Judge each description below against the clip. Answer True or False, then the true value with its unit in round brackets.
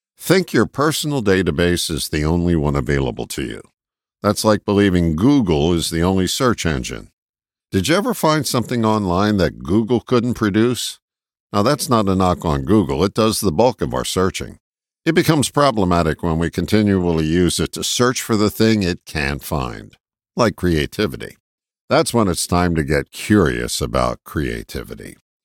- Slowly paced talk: False (165 wpm)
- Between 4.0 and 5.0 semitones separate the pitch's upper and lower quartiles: False (5.5 semitones)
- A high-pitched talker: False (95 Hz)